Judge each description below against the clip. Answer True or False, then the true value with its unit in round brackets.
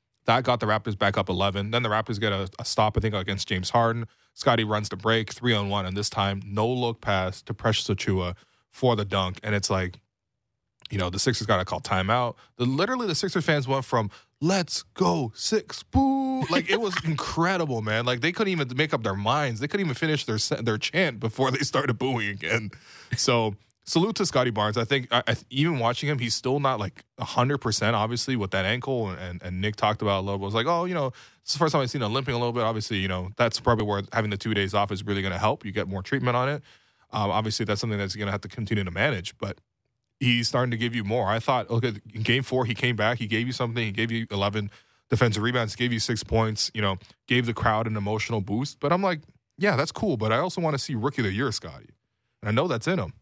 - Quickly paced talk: True (255 wpm)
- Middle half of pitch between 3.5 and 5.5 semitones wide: True (3.8 semitones)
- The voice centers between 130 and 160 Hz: False (115 Hz)